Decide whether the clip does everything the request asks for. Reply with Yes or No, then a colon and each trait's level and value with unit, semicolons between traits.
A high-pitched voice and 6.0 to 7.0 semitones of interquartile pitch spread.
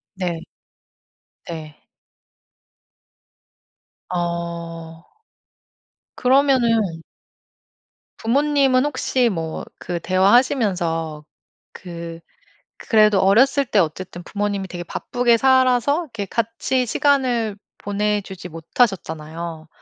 Yes: high, 200 Hz; wide, 6.5 semitones